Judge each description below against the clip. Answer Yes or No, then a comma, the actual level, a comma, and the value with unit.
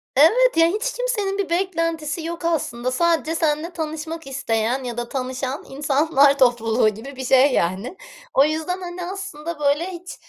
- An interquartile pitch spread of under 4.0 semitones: No, average, 4.5 semitones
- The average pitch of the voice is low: No, very high, 310 Hz